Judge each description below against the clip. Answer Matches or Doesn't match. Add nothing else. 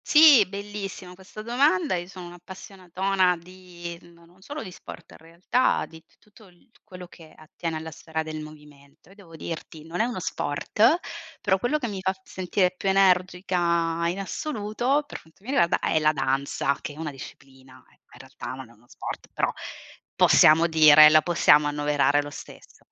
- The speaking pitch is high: Doesn't match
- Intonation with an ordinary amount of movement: Matches